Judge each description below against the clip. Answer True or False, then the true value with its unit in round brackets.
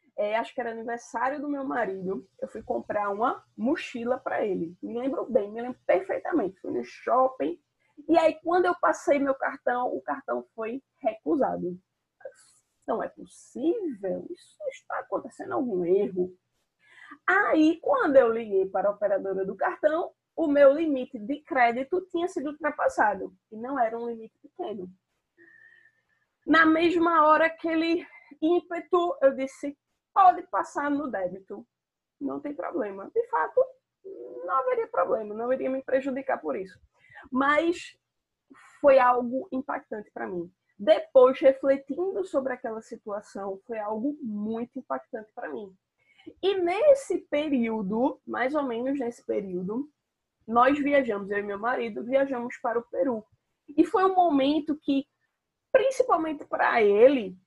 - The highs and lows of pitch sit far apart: True (5.9 semitones)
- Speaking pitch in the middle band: False (270 Hz)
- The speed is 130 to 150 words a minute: True (140 wpm)